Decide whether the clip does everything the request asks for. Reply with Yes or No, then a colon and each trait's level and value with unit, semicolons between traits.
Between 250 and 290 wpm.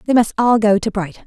Yes: fast, 285 wpm